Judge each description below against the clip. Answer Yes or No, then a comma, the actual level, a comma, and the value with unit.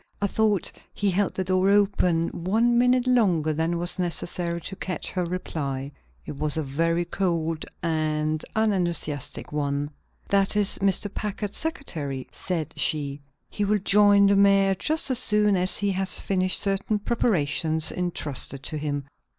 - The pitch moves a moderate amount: Yes, average, 4.4 semitones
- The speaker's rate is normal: Yes, average, 150 wpm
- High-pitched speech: No, medium, 180 Hz